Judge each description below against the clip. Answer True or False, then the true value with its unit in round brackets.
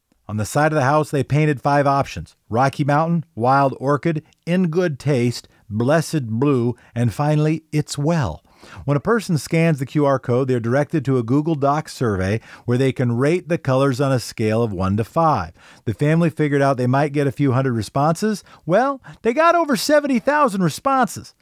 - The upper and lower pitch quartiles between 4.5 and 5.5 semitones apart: True (4.8 semitones)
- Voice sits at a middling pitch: True (145 Hz)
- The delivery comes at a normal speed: True (190 wpm)